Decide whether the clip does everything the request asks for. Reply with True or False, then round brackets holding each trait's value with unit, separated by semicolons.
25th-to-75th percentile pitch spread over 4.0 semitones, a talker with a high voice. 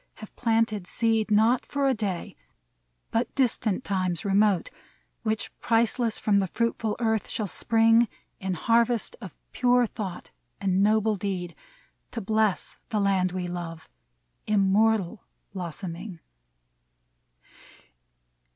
False (3.2 semitones; 215 Hz)